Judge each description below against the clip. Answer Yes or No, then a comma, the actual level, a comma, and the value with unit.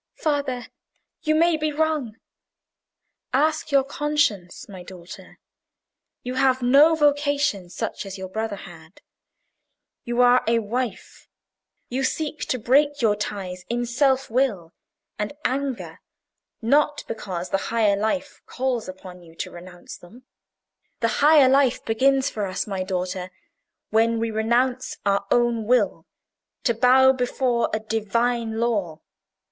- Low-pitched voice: No, high, 235 Hz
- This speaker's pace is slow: Yes, slow, 130 wpm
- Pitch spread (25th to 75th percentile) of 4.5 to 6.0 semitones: Yes, average, 5.1 semitones